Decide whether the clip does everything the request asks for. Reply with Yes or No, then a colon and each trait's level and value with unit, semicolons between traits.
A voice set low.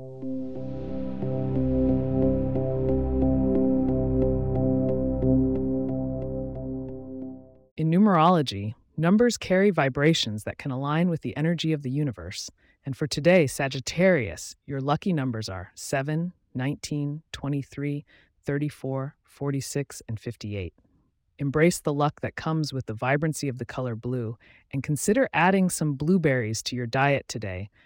Yes: low, 130 Hz